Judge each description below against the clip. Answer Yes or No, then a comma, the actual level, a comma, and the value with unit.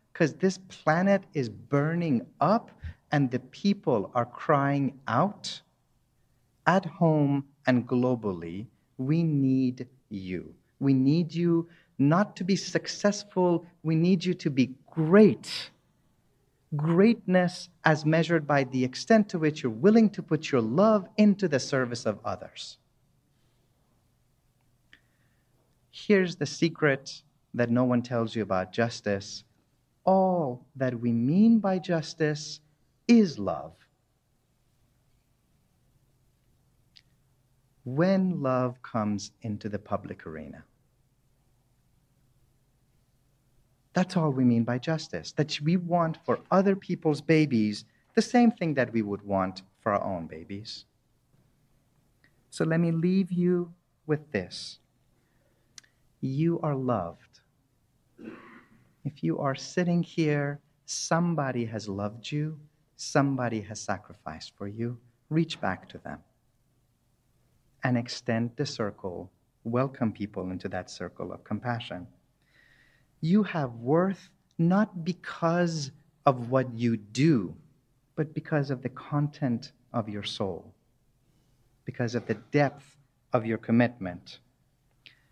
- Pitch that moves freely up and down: No, average, 4.8 semitones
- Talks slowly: Yes, slow, 115 wpm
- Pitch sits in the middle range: No, low, 130 Hz